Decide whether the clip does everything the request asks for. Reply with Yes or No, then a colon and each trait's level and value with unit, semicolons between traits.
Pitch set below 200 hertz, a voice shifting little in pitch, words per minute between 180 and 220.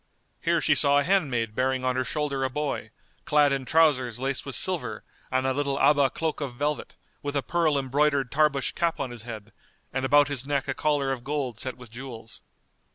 Yes: low, 135 Hz; narrow, 2.3 semitones; fast, 205 wpm